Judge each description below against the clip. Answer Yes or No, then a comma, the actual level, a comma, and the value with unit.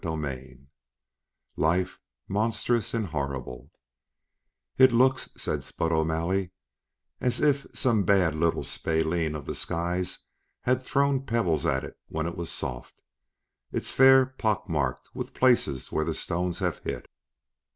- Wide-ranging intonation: Yes, wide, 6.9 semitones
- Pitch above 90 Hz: No, very low, 85 Hz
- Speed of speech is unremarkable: No, slow, 130 wpm